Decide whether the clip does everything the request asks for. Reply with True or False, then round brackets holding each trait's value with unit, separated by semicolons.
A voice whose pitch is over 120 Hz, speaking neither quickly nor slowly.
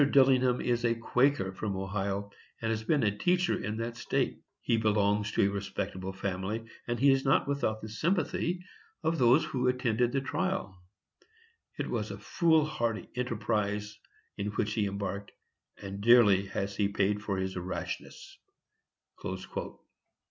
False (110 Hz; 150 wpm)